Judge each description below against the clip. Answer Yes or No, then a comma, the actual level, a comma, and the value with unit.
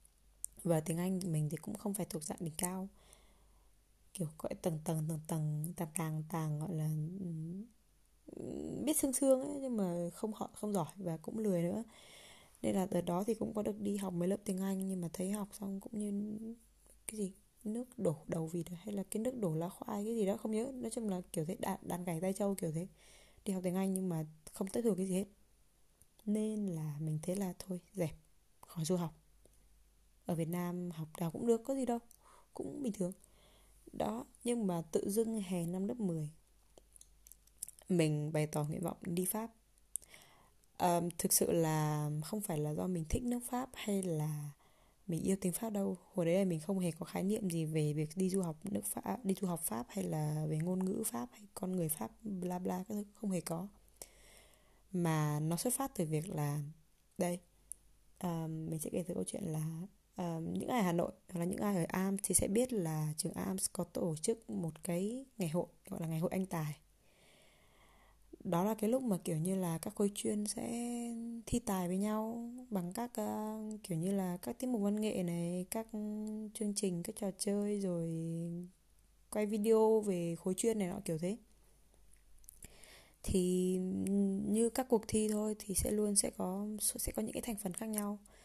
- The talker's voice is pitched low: No, medium, 185 Hz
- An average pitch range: Yes, average, 4.0 semitones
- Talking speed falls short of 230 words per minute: Yes, average, 205 wpm